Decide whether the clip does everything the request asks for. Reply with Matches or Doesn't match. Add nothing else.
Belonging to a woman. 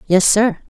Matches